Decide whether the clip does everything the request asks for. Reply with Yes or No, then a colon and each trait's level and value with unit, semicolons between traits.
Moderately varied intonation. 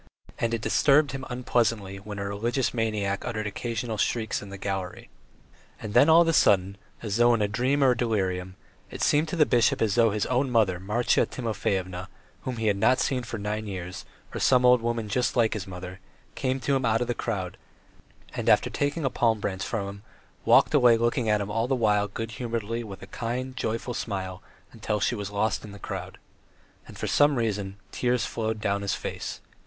Yes: average, 3.4 semitones